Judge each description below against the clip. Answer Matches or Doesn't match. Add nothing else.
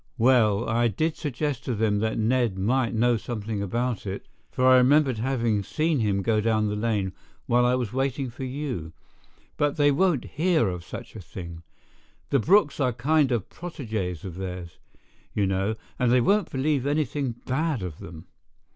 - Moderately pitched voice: Doesn't match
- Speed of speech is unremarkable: Matches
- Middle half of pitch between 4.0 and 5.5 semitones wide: Matches